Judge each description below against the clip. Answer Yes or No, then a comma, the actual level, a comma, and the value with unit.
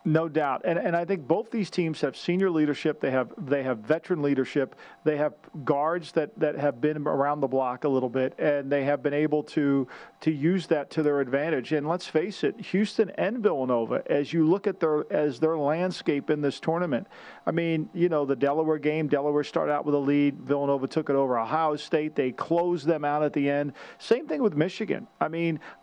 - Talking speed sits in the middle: No, fast, 215 wpm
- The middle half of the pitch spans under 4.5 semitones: Yes, narrow, 2.5 semitones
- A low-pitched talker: No, medium, 150 Hz